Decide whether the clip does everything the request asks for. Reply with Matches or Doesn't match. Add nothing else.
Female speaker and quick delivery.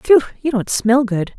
Matches